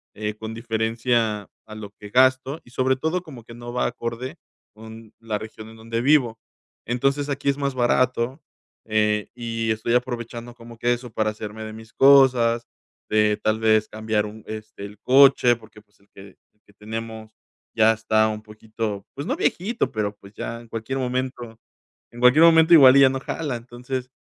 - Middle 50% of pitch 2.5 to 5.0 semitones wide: Yes, average, 2.9 semitones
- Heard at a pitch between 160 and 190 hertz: No, low, 115 Hz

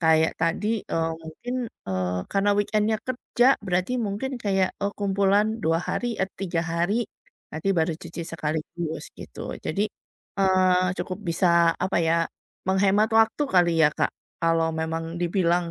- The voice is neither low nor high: Yes, medium, 180 Hz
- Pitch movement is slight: No, average, 3.7 semitones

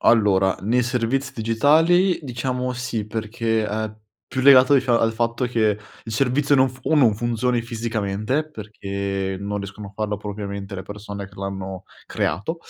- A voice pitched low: Yes, low, 110 Hz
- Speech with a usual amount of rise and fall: Yes, average, 3.7 semitones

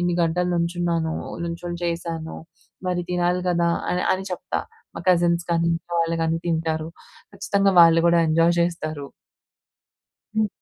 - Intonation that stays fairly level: Yes, narrow, 1.1 semitones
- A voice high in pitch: No, medium, 170 Hz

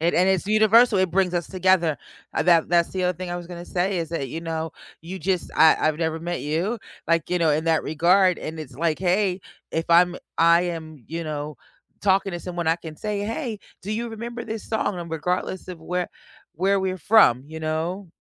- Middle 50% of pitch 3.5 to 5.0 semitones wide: No, average, 2.8 semitones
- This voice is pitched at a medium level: Yes, medium, 175 Hz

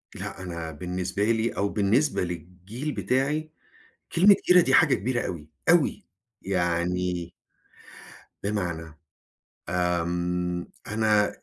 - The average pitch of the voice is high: No, very low, 90 Hz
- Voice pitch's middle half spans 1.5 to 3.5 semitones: No, average, 4.5 semitones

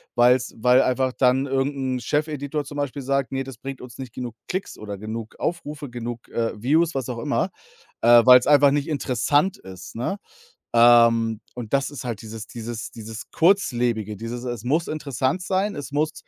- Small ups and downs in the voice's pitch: No, average, 3.5 semitones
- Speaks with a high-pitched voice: No, low, 125 Hz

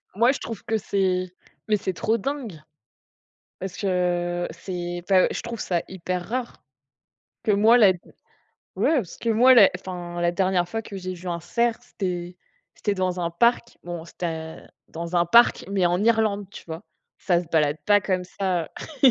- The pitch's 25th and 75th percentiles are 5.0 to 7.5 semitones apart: No, average, 3.8 semitones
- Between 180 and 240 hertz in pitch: Yes, medium, 185 Hz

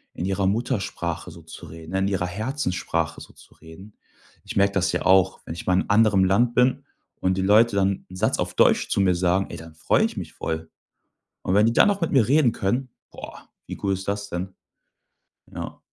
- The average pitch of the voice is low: Yes, very low, 95 Hz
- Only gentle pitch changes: No, average, 3.0 semitones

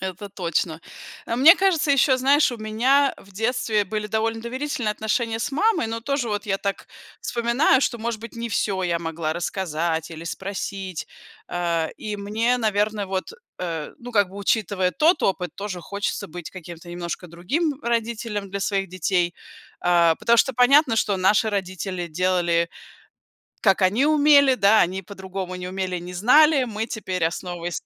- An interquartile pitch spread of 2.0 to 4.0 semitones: No, average, 4.6 semitones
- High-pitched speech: Yes, high, 205 Hz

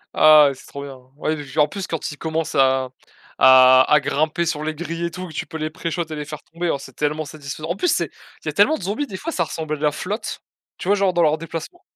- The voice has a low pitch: No, medium, 155 Hz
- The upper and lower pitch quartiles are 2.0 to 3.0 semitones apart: Yes, average, 2.7 semitones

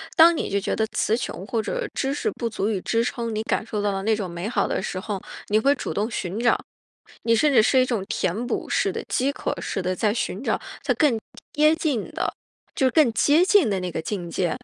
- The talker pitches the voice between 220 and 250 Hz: Yes, high, 225 Hz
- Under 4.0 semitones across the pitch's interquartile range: No, average, 5.0 semitones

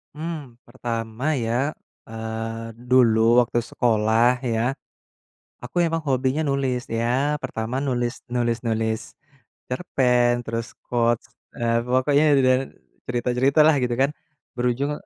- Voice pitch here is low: Yes, low, 125 Hz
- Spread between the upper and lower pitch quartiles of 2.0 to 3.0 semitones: Yes, narrow, 2.4 semitones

